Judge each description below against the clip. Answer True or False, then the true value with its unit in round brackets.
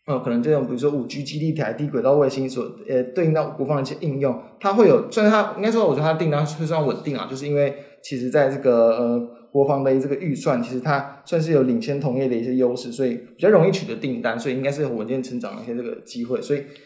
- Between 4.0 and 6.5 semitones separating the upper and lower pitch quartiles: False (2.7 semitones)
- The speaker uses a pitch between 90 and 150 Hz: True (140 Hz)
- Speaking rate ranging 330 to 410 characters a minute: True (400 characters per minute)